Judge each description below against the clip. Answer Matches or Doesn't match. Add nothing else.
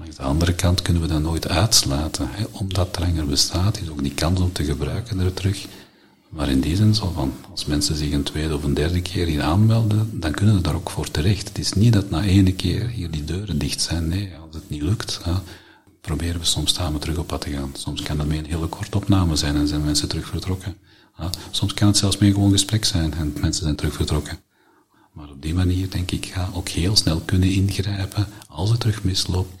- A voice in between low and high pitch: Doesn't match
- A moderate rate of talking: Doesn't match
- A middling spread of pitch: Matches